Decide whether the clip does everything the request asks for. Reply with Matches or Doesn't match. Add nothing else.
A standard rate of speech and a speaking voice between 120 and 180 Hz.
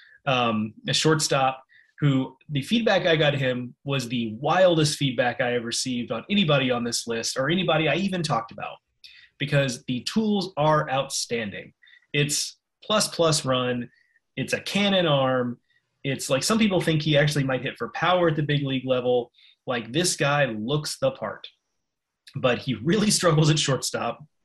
Matches